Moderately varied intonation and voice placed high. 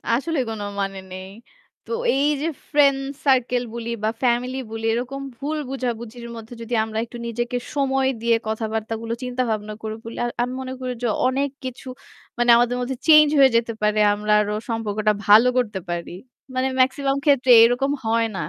Yes: average, 3.0 semitones; high, 240 Hz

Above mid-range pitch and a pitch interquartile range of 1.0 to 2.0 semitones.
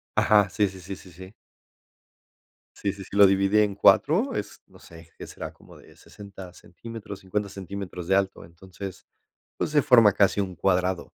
No: very low, 95 Hz; narrow, 1.7 semitones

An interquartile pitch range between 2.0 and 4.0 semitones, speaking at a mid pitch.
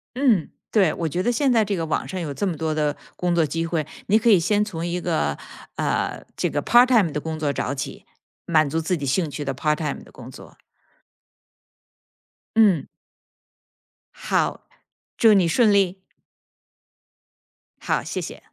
No: average, 4.7 semitones; medium, 170 Hz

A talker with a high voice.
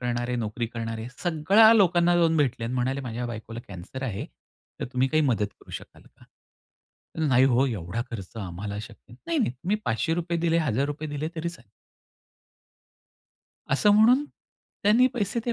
No: low, 135 Hz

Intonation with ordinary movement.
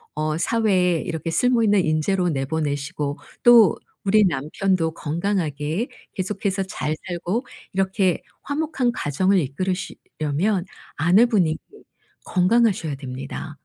Yes: average, 4.7 semitones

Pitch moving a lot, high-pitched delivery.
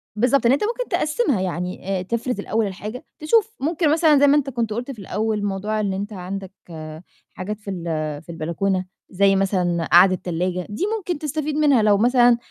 Yes: wide, 6.7 semitones; high, 215 Hz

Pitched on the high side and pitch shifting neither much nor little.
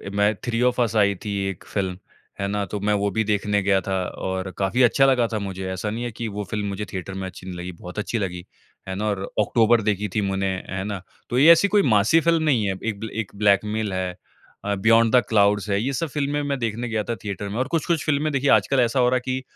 No: low, 105 Hz; average, 3.7 semitones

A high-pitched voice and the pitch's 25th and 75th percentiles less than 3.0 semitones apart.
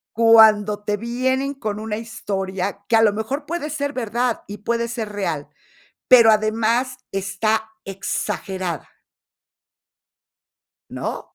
Yes: high, 220 Hz; narrow, 2.6 semitones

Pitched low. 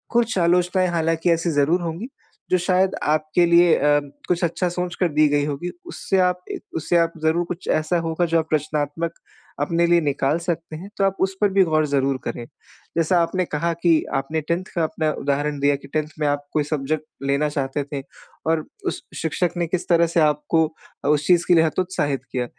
No: medium, 160 Hz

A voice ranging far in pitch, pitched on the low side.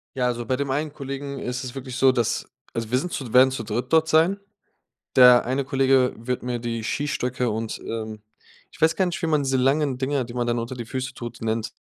No: narrow, 2.5 semitones; low, 130 Hz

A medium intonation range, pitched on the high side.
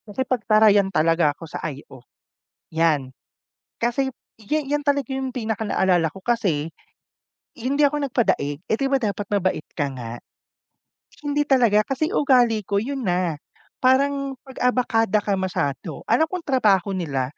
No: wide, 7.1 semitones; high, 215 Hz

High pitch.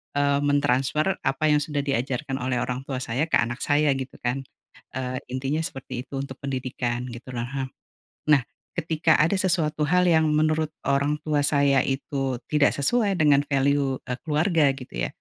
No: medium, 140 Hz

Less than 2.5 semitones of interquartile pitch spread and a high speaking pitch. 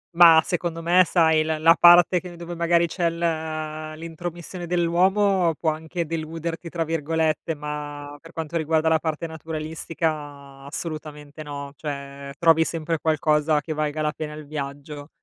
No: narrow, 1.8 semitones; medium, 160 Hz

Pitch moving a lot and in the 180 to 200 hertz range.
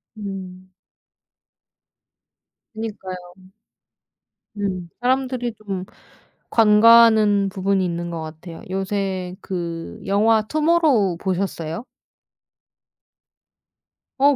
No: average, 3.4 semitones; high, 195 Hz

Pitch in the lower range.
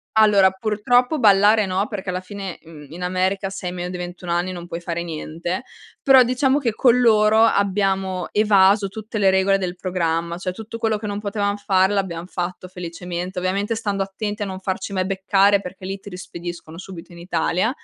No: high, 190 Hz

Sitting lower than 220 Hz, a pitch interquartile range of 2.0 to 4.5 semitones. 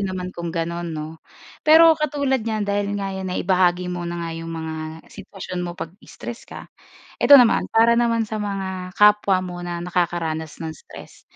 Yes: medium, 185 Hz; average, 3.4 semitones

